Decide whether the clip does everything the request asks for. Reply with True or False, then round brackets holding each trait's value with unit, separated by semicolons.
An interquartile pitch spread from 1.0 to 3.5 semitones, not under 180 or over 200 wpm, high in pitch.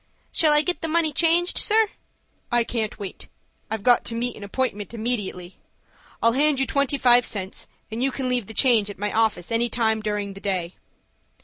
False (4.6 semitones; 195 wpm; 235 Hz)